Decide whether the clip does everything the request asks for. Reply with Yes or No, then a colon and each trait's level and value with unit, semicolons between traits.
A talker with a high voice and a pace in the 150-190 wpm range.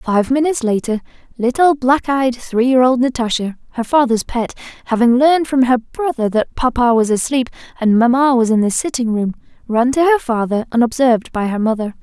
Yes: high, 245 Hz; average, 185 wpm